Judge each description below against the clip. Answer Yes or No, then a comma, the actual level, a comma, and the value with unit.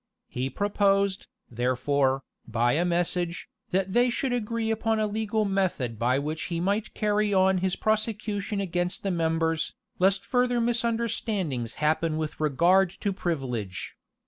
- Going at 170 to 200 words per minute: No, average, 140 wpm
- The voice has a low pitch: No, medium, 185 Hz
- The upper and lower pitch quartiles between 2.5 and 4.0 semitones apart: No, average, 5.3 semitones